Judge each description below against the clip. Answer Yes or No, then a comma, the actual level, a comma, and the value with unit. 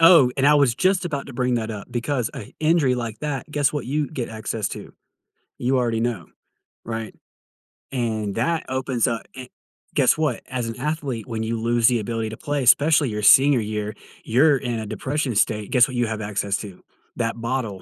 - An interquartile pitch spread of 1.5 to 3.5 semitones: No, average, 3.9 semitones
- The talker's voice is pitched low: Yes, low, 120 Hz